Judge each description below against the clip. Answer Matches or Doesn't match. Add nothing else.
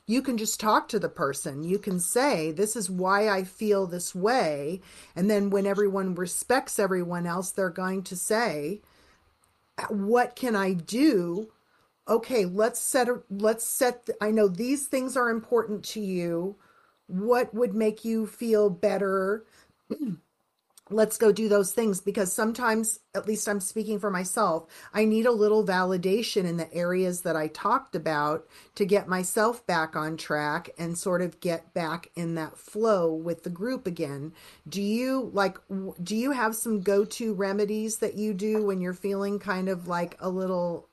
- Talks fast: Doesn't match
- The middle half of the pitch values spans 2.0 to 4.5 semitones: Matches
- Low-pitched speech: Doesn't match